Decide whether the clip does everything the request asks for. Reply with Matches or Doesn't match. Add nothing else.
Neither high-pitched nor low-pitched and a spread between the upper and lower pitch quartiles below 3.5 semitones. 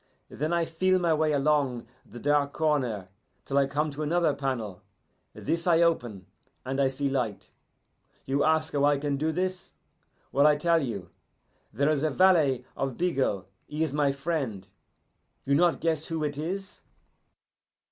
Matches